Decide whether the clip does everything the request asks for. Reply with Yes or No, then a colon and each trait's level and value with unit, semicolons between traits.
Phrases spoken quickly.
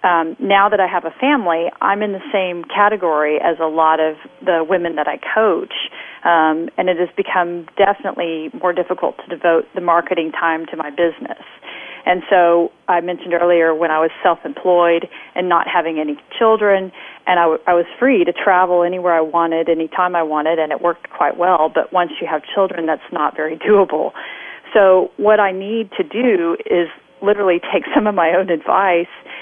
No: average, 190 wpm